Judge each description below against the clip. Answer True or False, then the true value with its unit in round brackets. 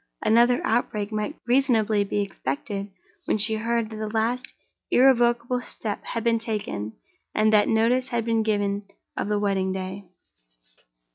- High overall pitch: True (220 Hz)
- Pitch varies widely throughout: False (2.5 semitones)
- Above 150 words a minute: False (145 wpm)